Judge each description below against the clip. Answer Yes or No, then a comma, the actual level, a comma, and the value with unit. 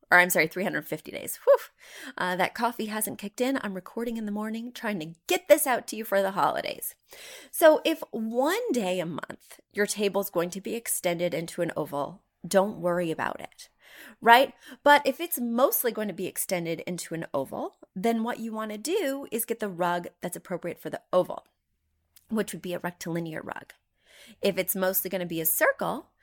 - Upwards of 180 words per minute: Yes, average, 200 wpm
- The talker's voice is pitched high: Yes, high, 205 Hz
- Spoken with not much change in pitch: No, average, 5.3 semitones